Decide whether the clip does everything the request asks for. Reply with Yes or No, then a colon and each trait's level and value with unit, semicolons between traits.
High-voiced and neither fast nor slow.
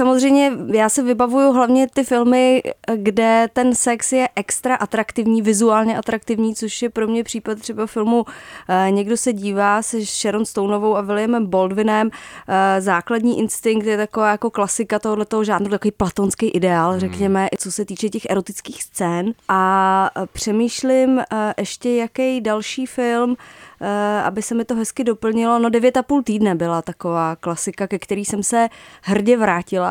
Yes: high, 220 Hz; average, 150 wpm